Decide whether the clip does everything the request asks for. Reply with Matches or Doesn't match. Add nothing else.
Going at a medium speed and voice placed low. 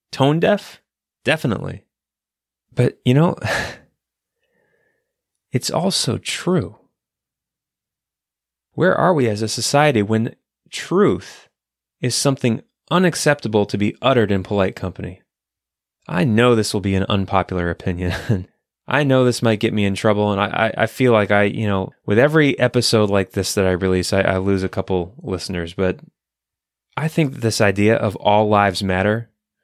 Matches